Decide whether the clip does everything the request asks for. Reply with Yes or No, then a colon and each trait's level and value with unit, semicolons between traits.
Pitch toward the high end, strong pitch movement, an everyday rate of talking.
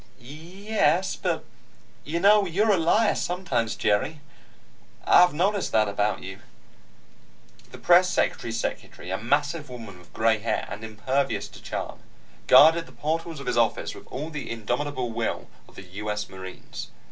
No: medium, 140 Hz; wide, 7.5 semitones; average, 160 wpm